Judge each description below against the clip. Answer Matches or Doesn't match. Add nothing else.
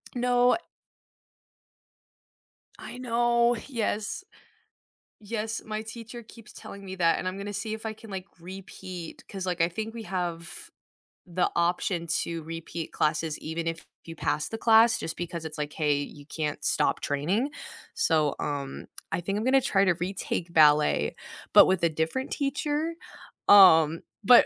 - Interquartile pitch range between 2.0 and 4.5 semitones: Doesn't match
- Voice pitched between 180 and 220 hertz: Matches